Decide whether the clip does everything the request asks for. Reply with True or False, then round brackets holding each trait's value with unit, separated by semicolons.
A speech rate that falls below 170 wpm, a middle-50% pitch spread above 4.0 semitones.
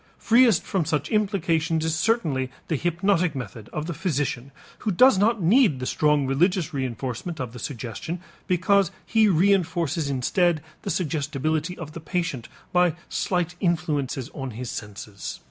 True (145 wpm; 4.9 semitones)